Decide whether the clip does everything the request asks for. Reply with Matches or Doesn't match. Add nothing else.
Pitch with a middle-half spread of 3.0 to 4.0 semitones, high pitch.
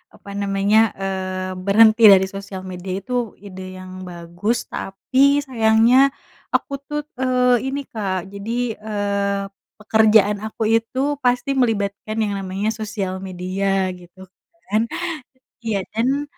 Matches